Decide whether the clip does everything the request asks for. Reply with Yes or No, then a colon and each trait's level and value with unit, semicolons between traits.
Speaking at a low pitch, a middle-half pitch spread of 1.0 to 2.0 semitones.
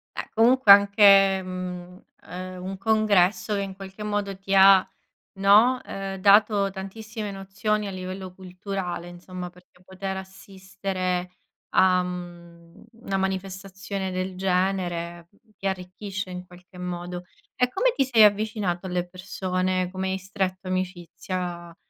No: high, 190 Hz; narrow, 1.6 semitones